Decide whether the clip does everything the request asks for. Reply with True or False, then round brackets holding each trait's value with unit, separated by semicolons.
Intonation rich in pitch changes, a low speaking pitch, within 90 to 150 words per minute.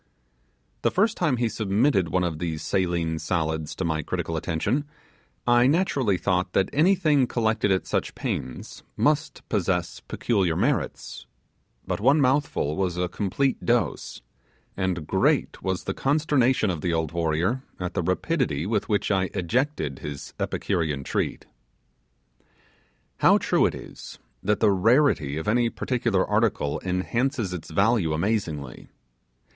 True (6.6 semitones; 95 Hz; 140 wpm)